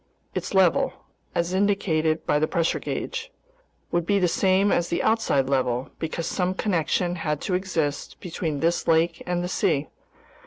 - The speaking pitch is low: No, medium, 175 Hz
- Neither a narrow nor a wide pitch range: Yes, average, 3.2 semitones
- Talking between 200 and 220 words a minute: No, average, 150 wpm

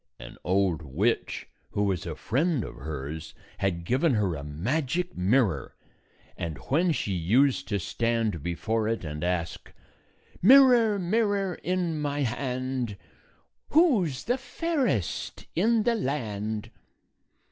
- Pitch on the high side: No, low, 120 Hz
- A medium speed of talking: No, slow, 125 wpm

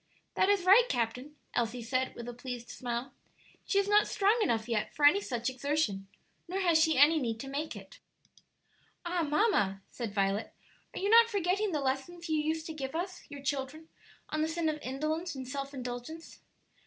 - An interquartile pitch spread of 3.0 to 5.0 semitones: No, wide, 5.6 semitones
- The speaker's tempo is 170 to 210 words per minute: Yes, average, 190 wpm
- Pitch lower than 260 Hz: No, very high, 295 Hz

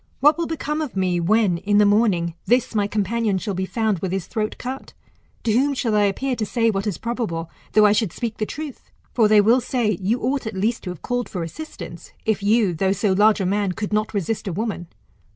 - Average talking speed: No, fast, 235 wpm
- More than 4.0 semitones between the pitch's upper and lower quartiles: No, average, 3.4 semitones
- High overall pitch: Yes, high, 215 Hz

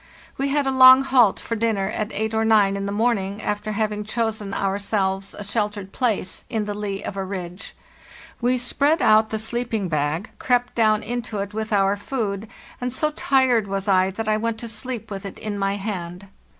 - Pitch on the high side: Yes, high, 215 Hz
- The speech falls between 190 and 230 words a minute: Yes, average, 200 wpm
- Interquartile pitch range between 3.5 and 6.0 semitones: No, average, 2.8 semitones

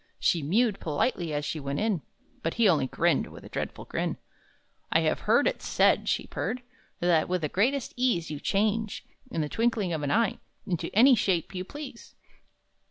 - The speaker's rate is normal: Yes, average, 185 wpm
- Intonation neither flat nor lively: No, wide, 6.3 semitones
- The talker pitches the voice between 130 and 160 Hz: No, medium, 185 Hz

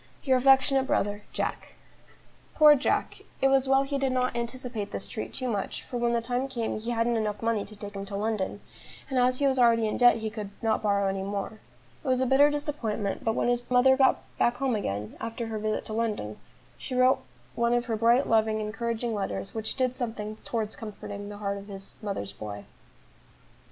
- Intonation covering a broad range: No, average, 3.4 semitones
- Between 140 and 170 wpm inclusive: No, fast, 205 wpm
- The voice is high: Yes, high, 230 Hz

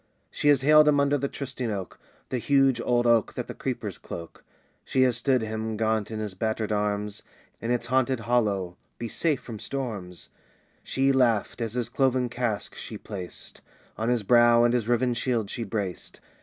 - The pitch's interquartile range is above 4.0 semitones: No, average, 3.1 semitones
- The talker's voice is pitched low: Yes, low, 120 Hz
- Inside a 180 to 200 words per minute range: Yes, average, 185 wpm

